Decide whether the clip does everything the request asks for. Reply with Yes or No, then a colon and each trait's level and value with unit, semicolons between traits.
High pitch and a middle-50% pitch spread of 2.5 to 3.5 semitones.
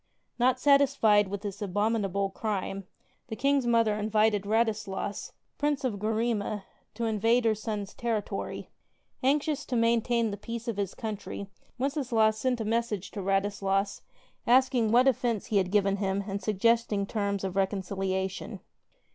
Yes: high, 215 Hz; average, 2.8 semitones